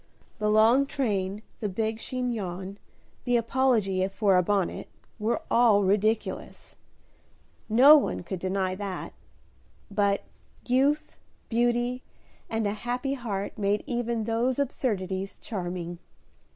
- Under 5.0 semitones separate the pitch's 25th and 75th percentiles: Yes, average, 3.8 semitones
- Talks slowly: Yes, slow, 110 wpm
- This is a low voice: No, high, 215 Hz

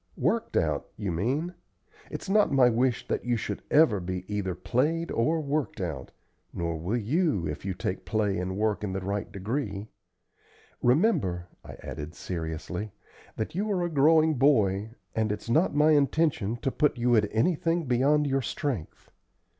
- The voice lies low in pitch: Yes, low, 115 Hz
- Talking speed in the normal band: Yes, average, 165 wpm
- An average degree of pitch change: No, wide, 7.6 semitones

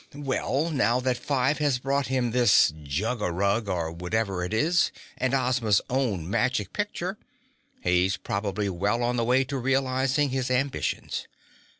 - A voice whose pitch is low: Yes, low, 125 Hz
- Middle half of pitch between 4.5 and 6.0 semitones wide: Yes, average, 4.9 semitones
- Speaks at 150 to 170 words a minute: Yes, average, 155 wpm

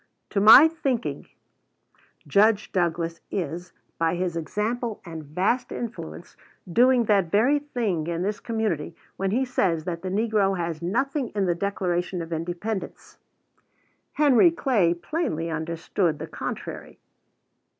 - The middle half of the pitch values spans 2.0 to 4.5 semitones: No, wide, 5.5 semitones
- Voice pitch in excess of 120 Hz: Yes, high, 190 Hz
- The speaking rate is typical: No, slow, 130 wpm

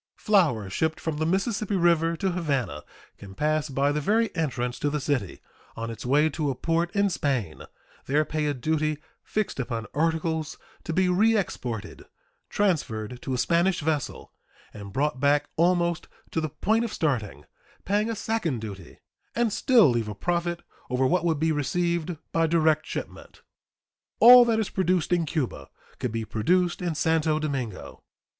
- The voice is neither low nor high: Yes, medium, 155 Hz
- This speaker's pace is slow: No, average, 165 wpm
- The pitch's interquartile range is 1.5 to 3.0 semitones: No, average, 5.1 semitones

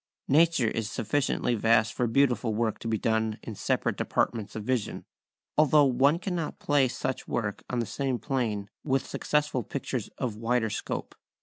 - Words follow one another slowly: No, average, 165 wpm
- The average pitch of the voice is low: Yes, low, 120 Hz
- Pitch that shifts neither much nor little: Yes, average, 3.8 semitones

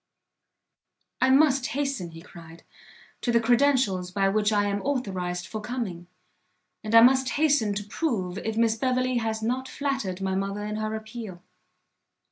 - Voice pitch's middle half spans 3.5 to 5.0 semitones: Yes, average, 4.7 semitones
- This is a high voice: Yes, high, 220 Hz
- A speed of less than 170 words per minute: Yes, average, 155 wpm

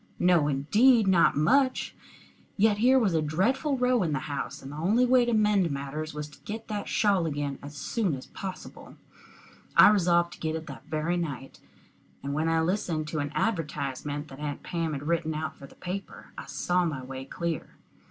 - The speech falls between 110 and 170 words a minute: No, average, 195 wpm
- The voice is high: No, medium, 165 Hz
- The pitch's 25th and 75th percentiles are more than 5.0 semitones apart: Yes, wide, 5.6 semitones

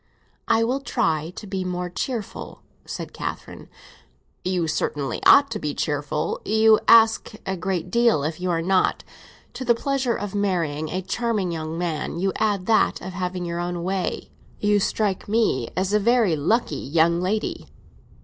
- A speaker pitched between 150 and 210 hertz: Yes, medium, 185 Hz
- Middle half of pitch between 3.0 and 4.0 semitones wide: No, average, 4.4 semitones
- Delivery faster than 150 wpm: Yes, average, 165 wpm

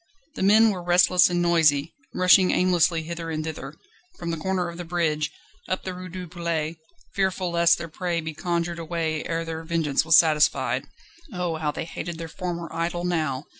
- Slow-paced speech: No, average, 185 wpm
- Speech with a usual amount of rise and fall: No, narrow, 1.8 semitones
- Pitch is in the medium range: Yes, medium, 170 Hz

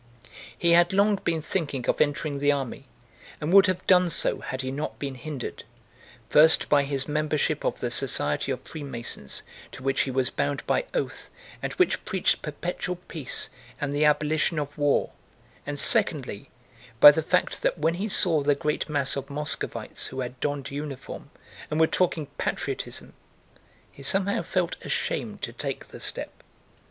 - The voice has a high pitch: No, medium, 150 Hz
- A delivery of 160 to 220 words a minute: Yes, average, 165 wpm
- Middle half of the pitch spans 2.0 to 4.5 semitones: Yes, average, 3.3 semitones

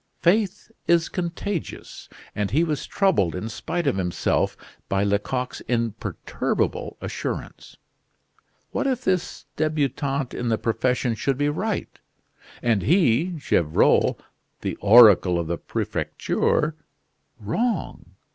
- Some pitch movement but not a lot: No, wide, 8.0 semitones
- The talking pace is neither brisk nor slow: No, slow, 110 wpm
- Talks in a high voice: No, low, 135 Hz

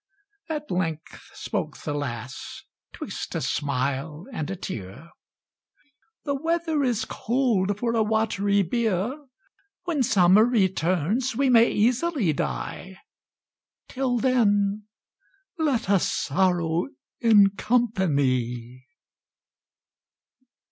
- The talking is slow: Yes, slow, 95 wpm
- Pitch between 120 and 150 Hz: No, high, 200 Hz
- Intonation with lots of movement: Yes, wide, 7.1 semitones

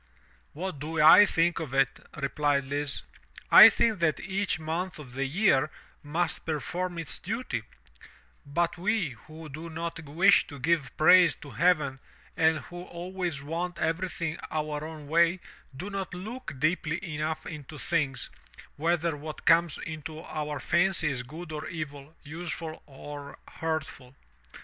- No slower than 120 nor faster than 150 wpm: Yes, average, 145 wpm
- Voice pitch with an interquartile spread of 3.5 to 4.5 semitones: No, average, 2.9 semitones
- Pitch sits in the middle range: Yes, medium, 160 Hz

